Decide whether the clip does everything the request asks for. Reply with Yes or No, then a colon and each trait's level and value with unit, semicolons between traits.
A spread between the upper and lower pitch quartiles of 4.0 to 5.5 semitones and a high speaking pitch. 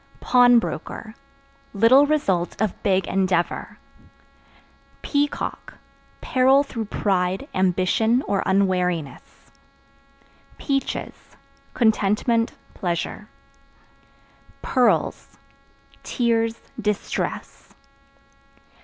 Yes: average, 4.7 semitones; high, 215 Hz